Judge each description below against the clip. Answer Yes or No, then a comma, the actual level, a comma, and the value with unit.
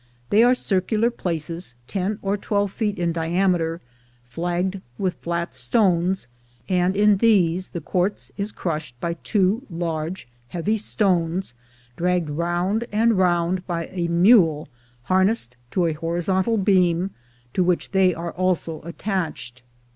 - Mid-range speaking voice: Yes, medium, 180 Hz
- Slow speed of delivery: Yes, slow, 130 wpm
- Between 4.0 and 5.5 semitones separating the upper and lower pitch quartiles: No, average, 2.7 semitones